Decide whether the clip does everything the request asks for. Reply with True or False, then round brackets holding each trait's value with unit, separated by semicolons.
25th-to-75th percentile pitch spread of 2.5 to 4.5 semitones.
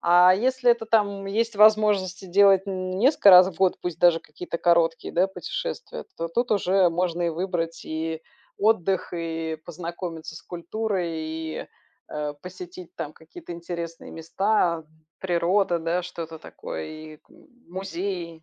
True (2.8 semitones)